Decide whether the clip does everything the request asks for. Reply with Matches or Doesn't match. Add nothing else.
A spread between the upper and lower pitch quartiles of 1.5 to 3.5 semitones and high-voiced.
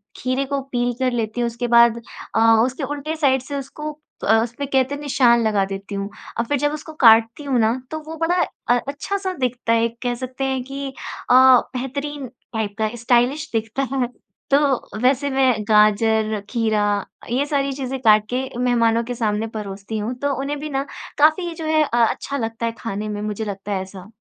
Doesn't match